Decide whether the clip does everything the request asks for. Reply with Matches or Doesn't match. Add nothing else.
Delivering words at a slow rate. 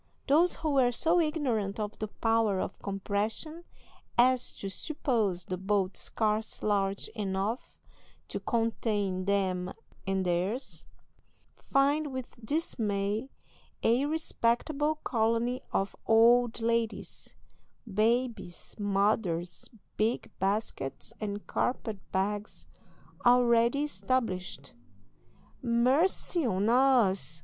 Matches